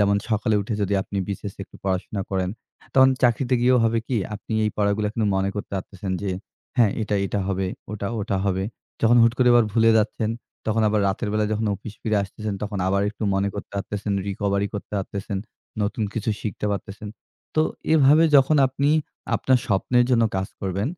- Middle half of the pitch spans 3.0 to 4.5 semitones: No, narrow, 2.5 semitones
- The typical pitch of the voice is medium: No, low, 105 Hz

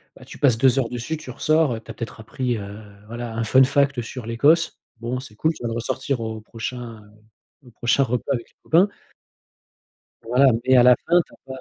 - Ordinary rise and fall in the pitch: Yes, average, 3.0 semitones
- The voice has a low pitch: Yes, low, 125 Hz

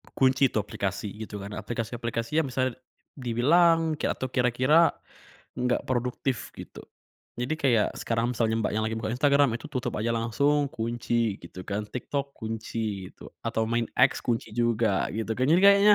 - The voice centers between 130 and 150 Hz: No, low, 120 Hz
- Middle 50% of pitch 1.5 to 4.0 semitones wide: Yes, average, 3.2 semitones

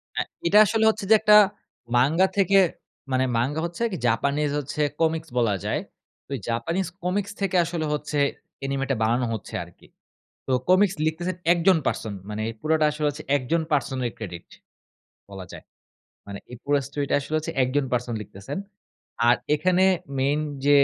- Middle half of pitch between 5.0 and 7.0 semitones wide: Yes, wide, 5.4 semitones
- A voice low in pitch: No, medium, 145 Hz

